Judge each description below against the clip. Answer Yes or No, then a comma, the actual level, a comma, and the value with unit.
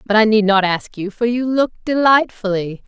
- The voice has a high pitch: Yes, high, 220 Hz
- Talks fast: Yes, fast, 210 wpm